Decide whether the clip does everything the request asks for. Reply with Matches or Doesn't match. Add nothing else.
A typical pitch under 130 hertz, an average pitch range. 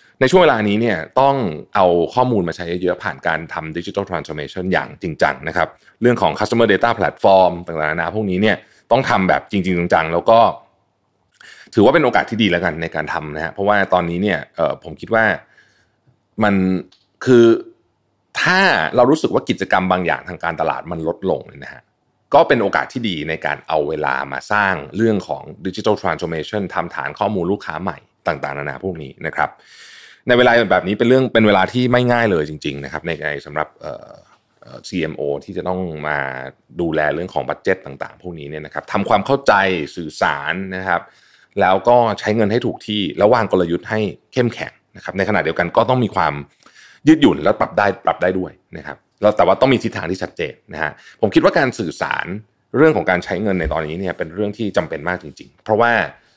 Matches